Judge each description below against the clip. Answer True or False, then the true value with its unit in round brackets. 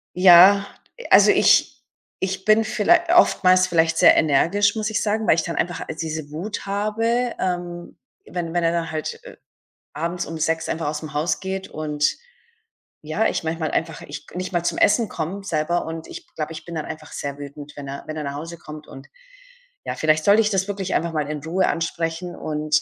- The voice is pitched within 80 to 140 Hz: False (170 Hz)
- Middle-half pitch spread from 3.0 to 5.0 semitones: True (3.6 semitones)